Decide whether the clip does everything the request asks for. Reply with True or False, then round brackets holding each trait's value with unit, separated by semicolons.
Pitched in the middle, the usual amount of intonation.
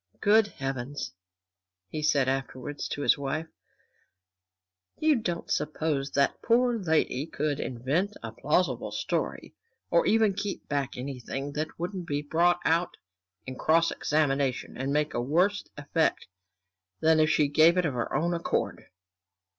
True (155 Hz; 4.0 semitones)